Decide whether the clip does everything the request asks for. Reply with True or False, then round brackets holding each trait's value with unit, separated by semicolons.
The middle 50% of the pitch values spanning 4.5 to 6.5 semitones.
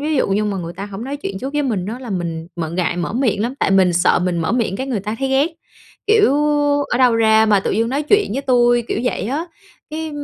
True (5.6 semitones)